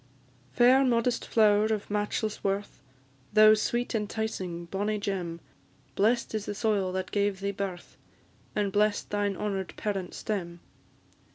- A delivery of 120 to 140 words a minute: Yes, slow, 135 wpm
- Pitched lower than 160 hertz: No, high, 205 Hz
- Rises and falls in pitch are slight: Yes, narrow, 1.9 semitones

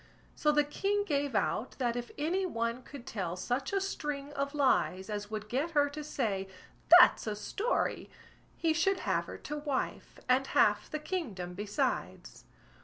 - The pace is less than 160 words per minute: No, average, 170 wpm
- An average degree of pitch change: No, wide, 5.8 semitones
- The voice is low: No, very high, 280 Hz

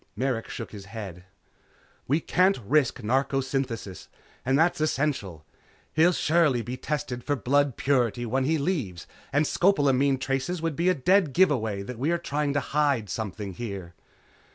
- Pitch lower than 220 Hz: Yes, low, 135 Hz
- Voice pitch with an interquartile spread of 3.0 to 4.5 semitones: No, average, 4.9 semitones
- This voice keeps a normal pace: Yes, average, 160 wpm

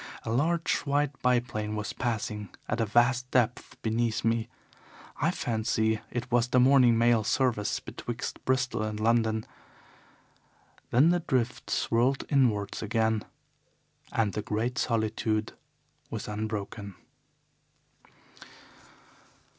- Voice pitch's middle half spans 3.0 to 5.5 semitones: No, narrow, 2.5 semitones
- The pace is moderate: No, slow, 110 wpm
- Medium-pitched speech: No, low, 115 Hz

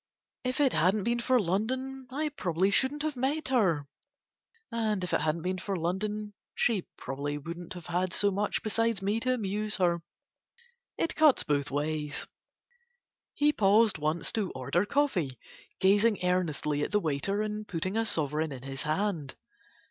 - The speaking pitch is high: Yes, high, 195 Hz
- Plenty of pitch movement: Yes, wide, 6.0 semitones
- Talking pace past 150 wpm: Yes, average, 160 wpm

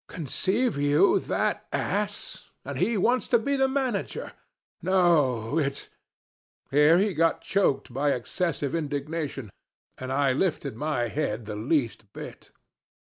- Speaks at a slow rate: Yes, slow, 130 wpm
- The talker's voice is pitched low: No, medium, 150 Hz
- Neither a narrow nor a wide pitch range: No, wide, 5.7 semitones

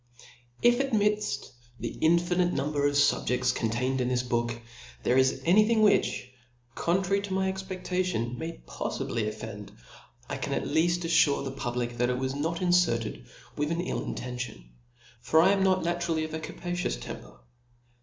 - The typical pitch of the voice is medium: Yes, medium, 155 Hz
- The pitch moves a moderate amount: No, wide, 6.7 semitones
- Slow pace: No, average, 170 wpm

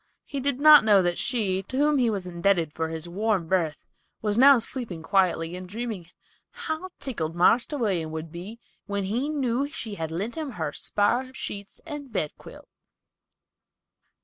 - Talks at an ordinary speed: Yes, average, 165 wpm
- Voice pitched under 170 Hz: No, high, 205 Hz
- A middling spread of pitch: No, wide, 6.9 semitones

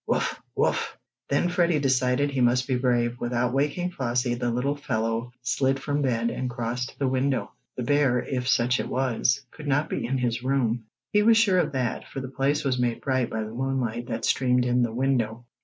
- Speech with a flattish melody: Yes, narrow, 2.2 semitones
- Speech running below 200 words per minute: No, fast, 205 wpm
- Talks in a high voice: No, low, 125 Hz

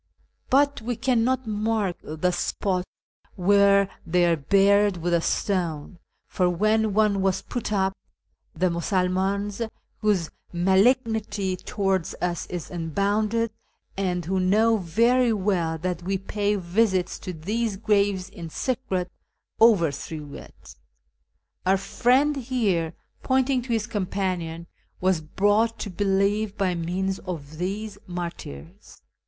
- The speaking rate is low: Yes, slow, 125 wpm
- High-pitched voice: Yes, high, 195 Hz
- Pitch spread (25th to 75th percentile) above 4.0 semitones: No, average, 3.4 semitones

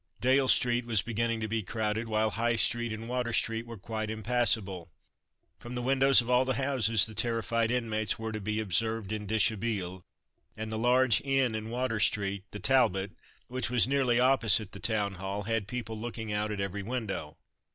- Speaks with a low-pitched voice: Yes, low, 110 Hz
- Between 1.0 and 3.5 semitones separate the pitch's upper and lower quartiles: Yes, narrow, 2.4 semitones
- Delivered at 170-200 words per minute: Yes, average, 185 wpm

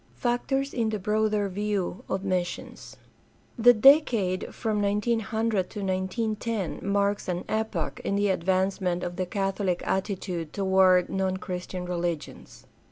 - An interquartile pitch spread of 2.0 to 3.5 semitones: Yes, average, 2.8 semitones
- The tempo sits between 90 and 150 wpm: Yes, average, 140 wpm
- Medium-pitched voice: No, high, 195 Hz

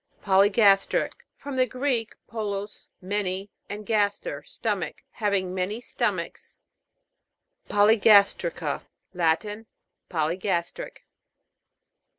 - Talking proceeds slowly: Yes, slow, 80 wpm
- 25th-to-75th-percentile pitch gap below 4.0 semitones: Yes, average, 2.7 semitones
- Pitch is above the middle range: Yes, high, 205 Hz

